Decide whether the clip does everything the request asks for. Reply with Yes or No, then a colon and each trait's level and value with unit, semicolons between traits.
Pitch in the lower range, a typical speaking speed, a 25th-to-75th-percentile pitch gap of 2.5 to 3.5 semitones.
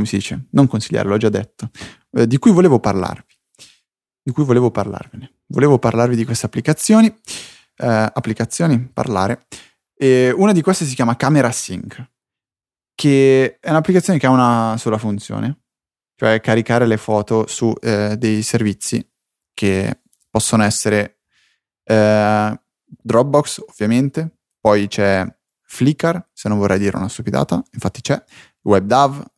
No: low, 115 Hz; average, 135 wpm; average, 4.2 semitones